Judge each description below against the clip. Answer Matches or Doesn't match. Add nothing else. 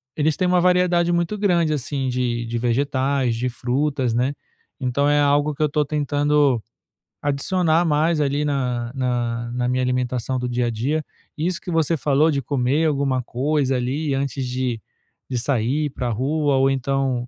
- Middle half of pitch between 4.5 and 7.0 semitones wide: Doesn't match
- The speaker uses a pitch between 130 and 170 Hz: Matches